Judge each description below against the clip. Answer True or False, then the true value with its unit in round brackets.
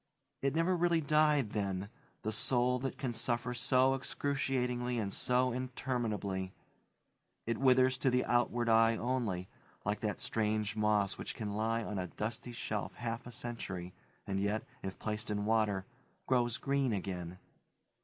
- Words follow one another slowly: False (150 wpm)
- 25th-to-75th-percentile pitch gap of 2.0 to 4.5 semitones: True (3.5 semitones)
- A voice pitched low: True (115 Hz)